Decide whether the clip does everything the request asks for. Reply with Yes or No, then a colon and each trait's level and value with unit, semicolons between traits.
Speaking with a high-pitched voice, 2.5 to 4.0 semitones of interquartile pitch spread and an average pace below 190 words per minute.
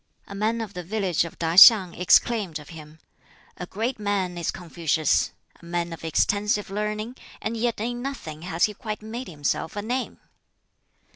No: high, 200 Hz; average, 4.5 semitones; average, 170 wpm